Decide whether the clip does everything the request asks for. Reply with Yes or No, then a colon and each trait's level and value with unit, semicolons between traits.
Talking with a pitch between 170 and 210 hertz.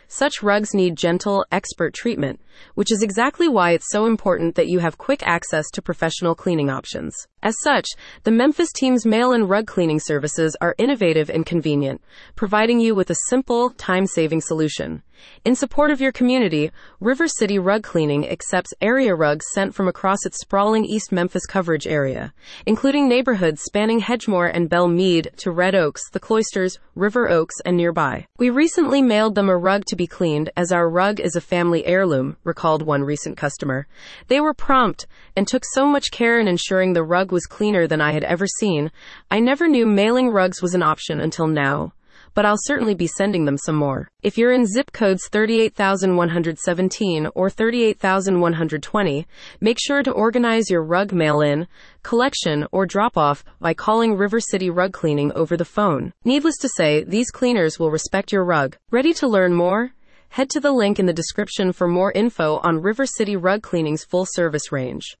Yes: high, 190 Hz